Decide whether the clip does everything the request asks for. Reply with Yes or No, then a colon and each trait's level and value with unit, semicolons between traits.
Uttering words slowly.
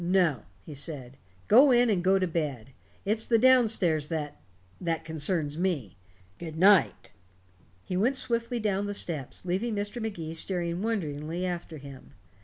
No: average, 155 wpm